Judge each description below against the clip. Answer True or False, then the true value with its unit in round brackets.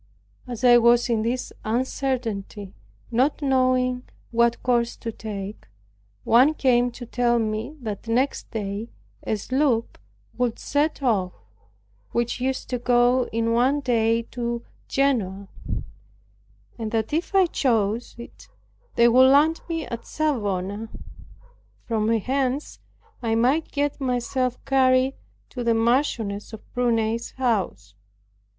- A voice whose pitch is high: True (240 Hz)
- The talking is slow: True (125 wpm)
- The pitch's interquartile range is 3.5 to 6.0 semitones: False (2.5 semitones)